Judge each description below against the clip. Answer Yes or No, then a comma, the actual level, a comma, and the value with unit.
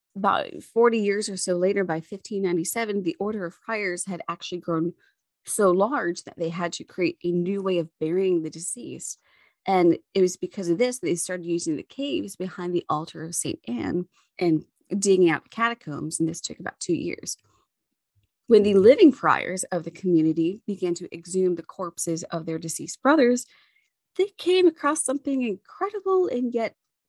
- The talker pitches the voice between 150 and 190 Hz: Yes, medium, 185 Hz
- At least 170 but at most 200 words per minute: Yes, average, 180 wpm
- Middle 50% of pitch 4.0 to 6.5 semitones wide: Yes, average, 5.1 semitones